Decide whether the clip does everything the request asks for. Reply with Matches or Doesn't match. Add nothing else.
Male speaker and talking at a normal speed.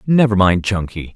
Matches